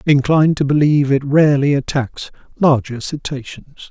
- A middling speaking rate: No, slow, 125 wpm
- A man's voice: Yes, male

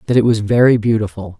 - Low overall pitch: Yes, low, 110 Hz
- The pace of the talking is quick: No, average, 170 wpm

